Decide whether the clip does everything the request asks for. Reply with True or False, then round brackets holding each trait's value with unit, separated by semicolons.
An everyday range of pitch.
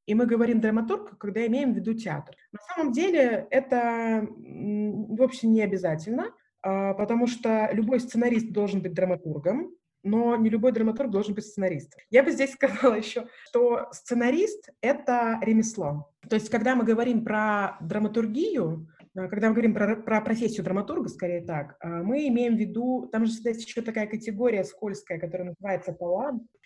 True (3.2 semitones)